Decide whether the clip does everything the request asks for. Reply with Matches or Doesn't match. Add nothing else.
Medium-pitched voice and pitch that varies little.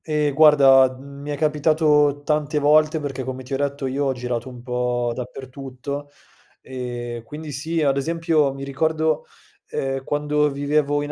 Matches